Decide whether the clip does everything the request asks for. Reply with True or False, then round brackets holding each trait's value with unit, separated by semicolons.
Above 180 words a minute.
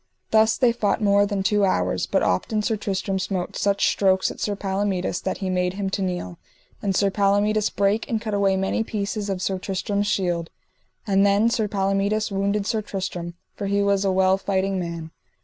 True (195 wpm)